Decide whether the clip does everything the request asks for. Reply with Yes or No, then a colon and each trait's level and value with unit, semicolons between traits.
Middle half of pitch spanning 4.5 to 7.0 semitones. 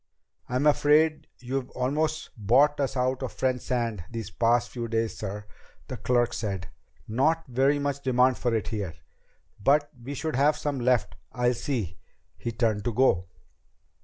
No: average, 3.6 semitones